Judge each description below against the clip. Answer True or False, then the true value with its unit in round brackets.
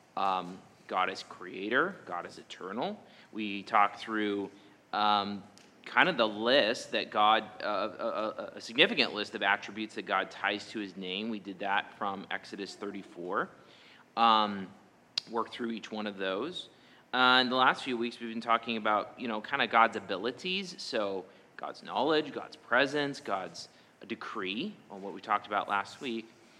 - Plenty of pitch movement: False (2.4 semitones)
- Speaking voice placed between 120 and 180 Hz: False (105 Hz)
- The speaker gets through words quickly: False (170 wpm)